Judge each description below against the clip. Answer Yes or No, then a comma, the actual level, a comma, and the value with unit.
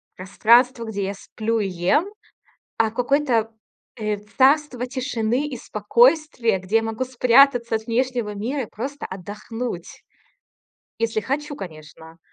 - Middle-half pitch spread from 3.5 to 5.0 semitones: Yes, average, 3.8 semitones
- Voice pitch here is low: No, high, 230 Hz